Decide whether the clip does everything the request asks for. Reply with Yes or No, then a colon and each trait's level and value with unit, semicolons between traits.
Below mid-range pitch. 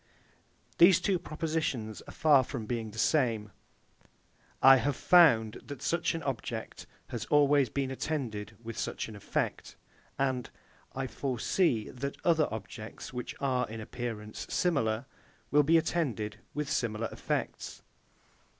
Yes: low, 130 Hz